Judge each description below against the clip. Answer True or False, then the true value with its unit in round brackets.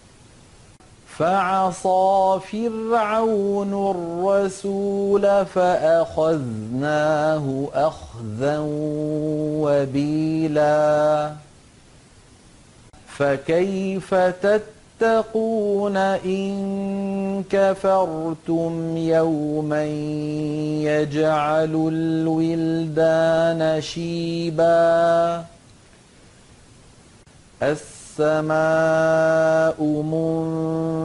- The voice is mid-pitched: True (160 Hz)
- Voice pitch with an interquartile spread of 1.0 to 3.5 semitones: False (4.0 semitones)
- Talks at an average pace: False (30 wpm)